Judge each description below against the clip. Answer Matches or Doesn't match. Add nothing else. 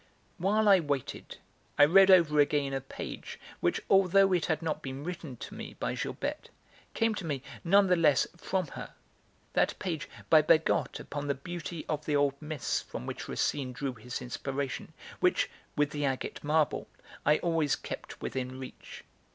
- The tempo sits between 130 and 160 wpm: Doesn't match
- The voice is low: Doesn't match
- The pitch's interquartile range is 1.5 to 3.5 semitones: Doesn't match